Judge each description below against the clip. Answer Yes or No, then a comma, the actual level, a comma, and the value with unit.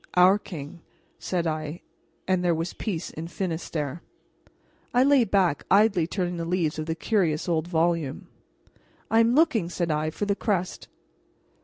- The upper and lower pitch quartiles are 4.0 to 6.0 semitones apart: No, average, 3.5 semitones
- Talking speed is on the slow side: No, average, 155 wpm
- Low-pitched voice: No, medium, 175 Hz